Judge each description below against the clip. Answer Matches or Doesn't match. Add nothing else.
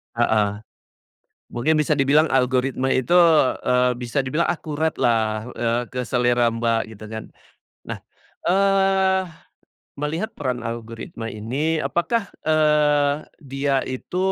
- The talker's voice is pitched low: Matches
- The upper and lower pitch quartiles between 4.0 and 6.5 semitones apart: Matches